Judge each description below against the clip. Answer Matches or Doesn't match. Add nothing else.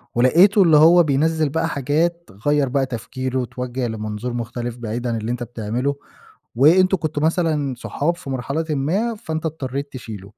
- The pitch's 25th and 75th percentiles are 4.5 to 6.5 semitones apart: Matches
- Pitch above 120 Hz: Matches